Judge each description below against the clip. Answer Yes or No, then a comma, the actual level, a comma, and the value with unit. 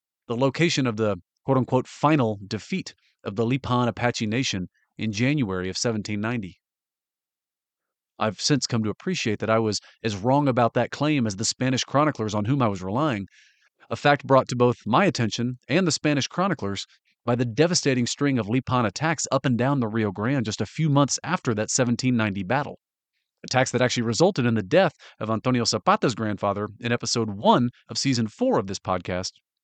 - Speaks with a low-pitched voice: Yes, low, 120 Hz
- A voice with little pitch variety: No, average, 3.8 semitones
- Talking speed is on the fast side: No, average, 185 wpm